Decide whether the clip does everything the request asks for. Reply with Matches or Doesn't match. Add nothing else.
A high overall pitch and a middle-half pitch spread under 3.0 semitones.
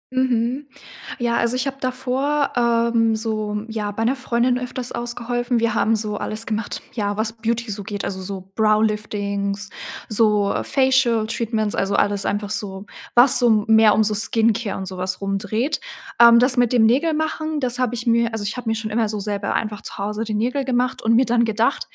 Matches